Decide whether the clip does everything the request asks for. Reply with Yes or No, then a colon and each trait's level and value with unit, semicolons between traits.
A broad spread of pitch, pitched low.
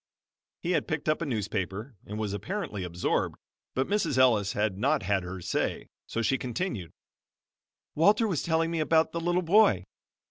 Yes: wide, 8.5 semitones; low, 130 Hz